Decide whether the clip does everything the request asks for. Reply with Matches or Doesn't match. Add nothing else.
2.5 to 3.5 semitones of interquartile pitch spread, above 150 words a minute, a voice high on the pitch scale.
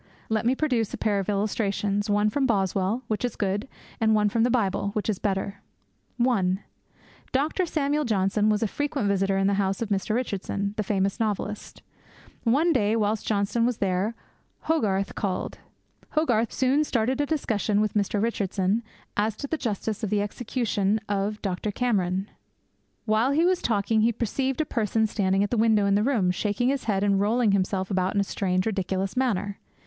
Matches